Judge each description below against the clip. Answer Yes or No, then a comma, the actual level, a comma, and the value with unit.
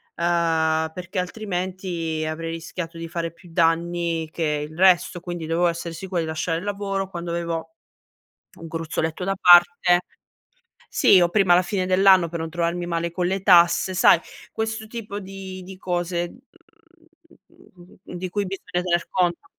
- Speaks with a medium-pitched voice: Yes, medium, 175 Hz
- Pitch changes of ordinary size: No, narrow, 2.1 semitones